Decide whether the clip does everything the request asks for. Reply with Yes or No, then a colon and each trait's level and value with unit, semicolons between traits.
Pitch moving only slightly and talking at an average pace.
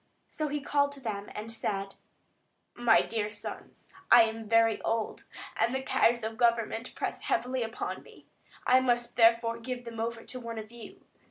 Yes: narrow, 1.8 semitones; average, 180 wpm